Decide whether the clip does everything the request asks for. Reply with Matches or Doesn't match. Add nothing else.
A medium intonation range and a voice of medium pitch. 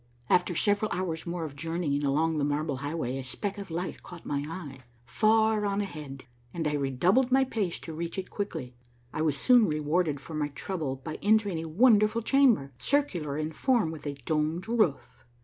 Doesn't match